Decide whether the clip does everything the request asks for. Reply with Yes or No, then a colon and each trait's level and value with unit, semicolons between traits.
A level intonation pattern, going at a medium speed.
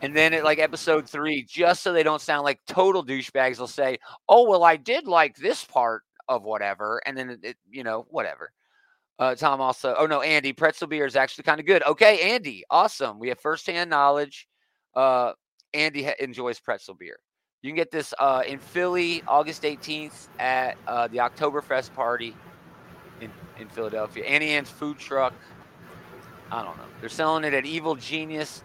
No: average, 3.2 semitones; average, 185 wpm